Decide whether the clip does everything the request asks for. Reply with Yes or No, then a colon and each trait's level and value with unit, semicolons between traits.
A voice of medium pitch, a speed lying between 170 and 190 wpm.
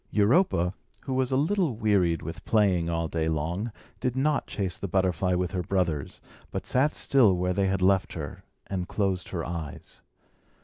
No: very low, 95 Hz; average, 175 wpm